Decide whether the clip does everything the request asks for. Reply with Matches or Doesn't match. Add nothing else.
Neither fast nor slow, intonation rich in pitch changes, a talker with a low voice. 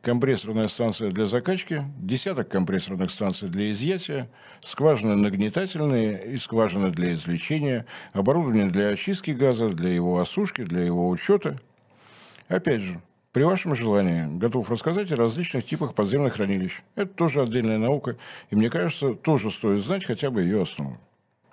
Matches